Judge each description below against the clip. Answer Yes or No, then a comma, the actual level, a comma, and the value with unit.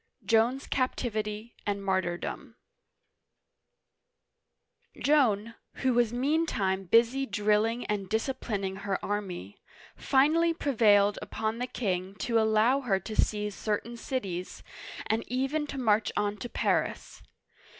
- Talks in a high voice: Yes, high, 220 Hz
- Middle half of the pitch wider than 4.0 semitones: No, average, 3.7 semitones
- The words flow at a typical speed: No, slow, 115 wpm